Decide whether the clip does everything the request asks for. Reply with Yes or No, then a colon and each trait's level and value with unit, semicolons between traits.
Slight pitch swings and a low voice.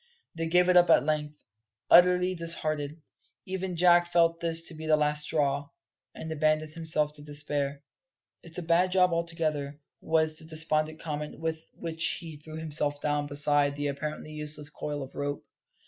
No: narrow, 2.1 semitones; medium, 155 Hz